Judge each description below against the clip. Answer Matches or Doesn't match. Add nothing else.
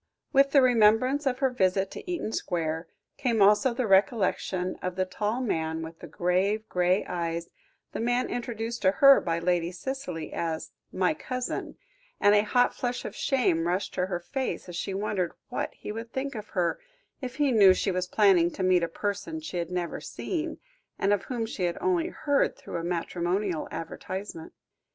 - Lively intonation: Matches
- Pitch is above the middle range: Matches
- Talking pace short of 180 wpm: Doesn't match